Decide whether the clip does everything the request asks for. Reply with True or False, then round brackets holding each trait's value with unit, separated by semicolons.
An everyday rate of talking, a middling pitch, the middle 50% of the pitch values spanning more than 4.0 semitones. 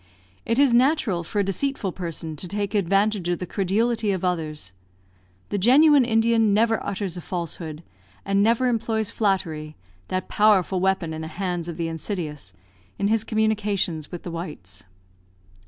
False (155 wpm; 195 Hz; 4.5 semitones)